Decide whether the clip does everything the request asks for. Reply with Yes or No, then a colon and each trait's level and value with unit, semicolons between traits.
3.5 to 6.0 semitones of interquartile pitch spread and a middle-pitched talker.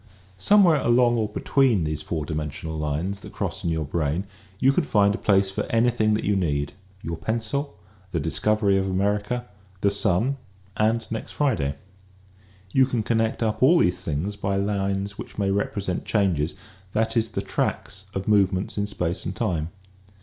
No: average, 4.2 semitones; low, 100 Hz